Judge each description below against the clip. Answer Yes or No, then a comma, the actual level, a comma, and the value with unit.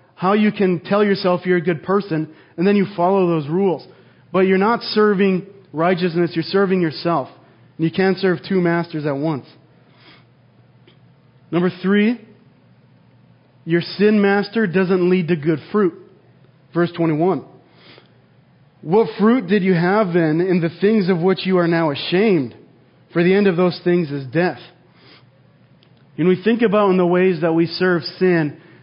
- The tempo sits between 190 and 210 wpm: No, average, 160 wpm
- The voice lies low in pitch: No, medium, 180 Hz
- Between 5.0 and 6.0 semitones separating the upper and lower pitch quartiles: No, average, 2.9 semitones